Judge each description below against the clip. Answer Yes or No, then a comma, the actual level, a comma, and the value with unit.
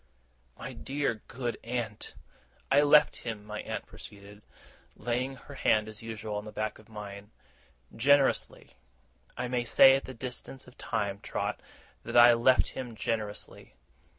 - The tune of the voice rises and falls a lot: No, average, 3.2 semitones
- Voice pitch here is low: Yes, low, 115 Hz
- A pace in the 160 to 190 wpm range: No, average, 150 wpm